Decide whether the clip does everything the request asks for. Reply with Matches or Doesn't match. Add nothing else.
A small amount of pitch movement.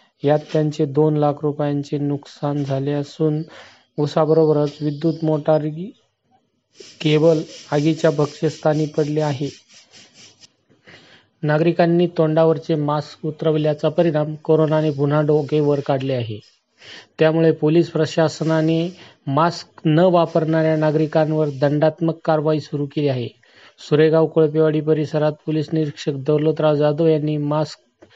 Matches